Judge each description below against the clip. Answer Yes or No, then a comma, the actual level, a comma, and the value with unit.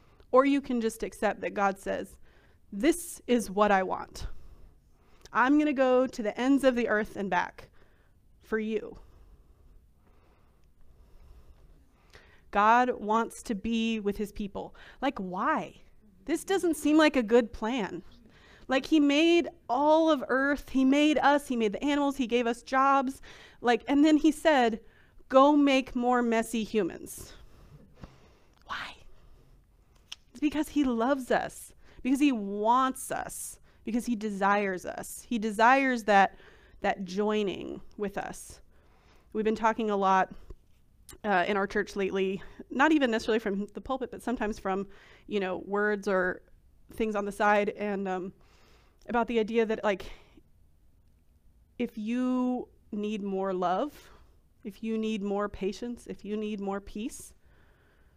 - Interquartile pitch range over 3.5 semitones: Yes, average, 5.1 semitones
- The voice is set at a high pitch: Yes, high, 220 Hz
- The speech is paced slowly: No, average, 145 wpm